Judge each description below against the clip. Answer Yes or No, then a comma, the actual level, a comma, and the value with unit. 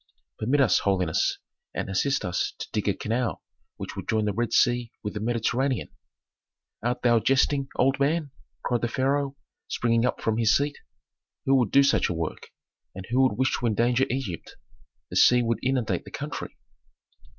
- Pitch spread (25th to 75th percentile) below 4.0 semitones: Yes, average, 3.4 semitones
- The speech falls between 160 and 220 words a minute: Yes, average, 175 wpm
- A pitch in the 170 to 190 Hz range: No, low, 120 Hz